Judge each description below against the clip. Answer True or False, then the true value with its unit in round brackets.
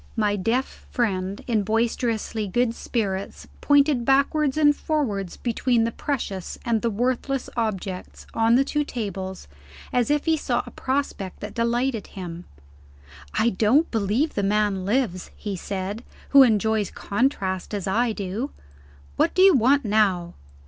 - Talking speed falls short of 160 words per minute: True (145 wpm)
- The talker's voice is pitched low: False (225 Hz)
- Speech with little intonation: False (4.6 semitones)